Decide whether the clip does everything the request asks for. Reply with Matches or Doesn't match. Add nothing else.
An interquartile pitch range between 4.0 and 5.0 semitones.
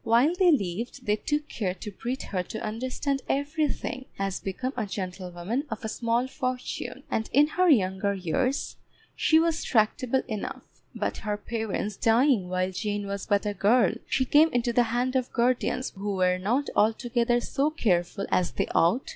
Matches